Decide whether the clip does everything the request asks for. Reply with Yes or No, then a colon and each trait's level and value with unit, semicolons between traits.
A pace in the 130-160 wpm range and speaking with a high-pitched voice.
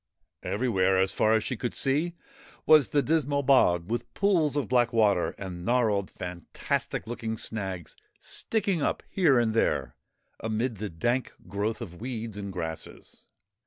No: average, 150 wpm; low, 115 Hz